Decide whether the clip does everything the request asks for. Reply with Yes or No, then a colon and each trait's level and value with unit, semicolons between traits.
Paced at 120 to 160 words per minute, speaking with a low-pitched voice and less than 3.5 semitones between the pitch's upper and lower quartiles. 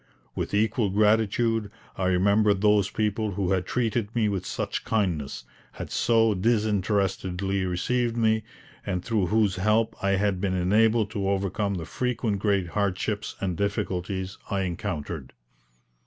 Yes: average, 140 wpm; low, 100 Hz; average, 2.7 semitones